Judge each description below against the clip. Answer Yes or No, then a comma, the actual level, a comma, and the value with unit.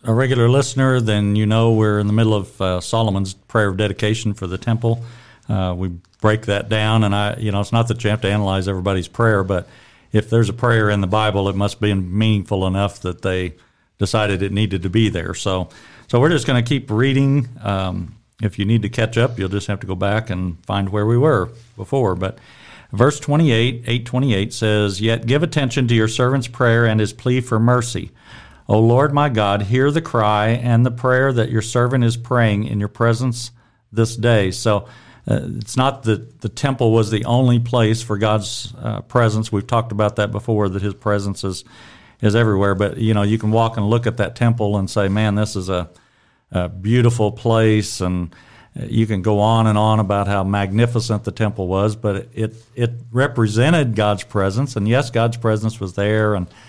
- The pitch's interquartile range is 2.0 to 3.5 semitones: Yes, average, 2.7 semitones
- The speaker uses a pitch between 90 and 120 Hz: Yes, low, 110 Hz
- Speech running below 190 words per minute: No, fast, 205 wpm